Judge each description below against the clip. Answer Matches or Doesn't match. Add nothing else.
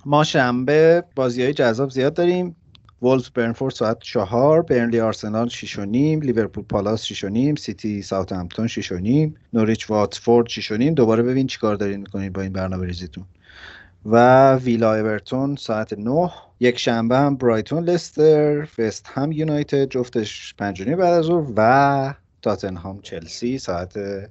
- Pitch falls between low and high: Doesn't match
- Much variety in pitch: Doesn't match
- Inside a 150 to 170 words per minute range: Matches